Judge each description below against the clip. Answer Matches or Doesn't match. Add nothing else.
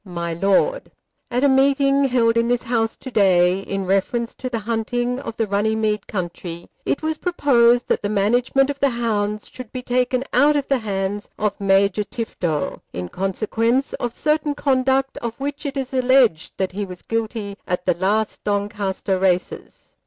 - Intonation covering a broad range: Doesn't match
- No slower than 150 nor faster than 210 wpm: Matches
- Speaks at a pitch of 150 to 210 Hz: Doesn't match